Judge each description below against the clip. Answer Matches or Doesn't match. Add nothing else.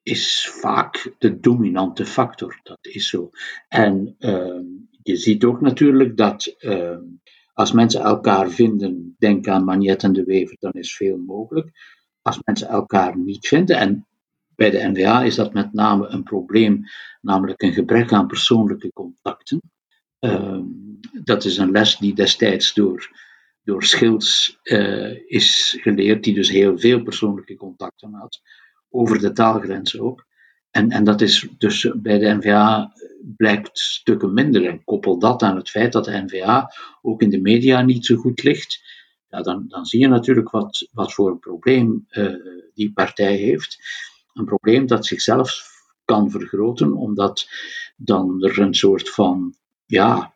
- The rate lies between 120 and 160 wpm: Matches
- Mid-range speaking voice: Doesn't match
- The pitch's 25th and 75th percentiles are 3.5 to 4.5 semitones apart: Matches